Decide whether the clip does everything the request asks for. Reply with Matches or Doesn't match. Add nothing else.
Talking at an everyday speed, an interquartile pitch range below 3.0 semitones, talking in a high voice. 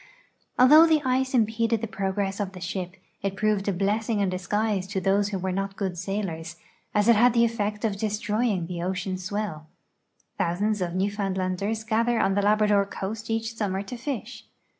Matches